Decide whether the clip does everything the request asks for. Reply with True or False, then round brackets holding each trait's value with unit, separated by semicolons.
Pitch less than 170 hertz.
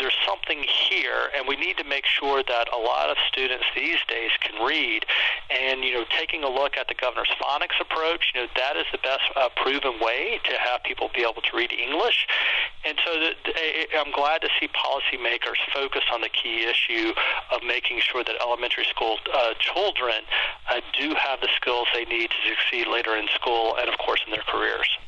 True (135 Hz)